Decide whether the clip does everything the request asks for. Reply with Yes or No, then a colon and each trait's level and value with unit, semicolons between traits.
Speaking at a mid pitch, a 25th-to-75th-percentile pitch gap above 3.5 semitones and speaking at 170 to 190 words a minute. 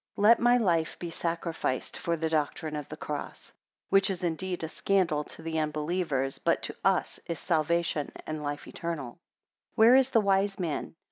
Yes: medium, 170 Hz; average, 3.9 semitones; average, 185 wpm